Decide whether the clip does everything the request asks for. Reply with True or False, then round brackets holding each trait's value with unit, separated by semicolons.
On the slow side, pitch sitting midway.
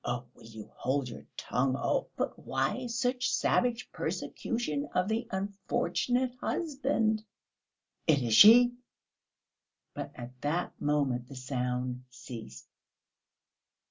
True (110 wpm; 150 Hz)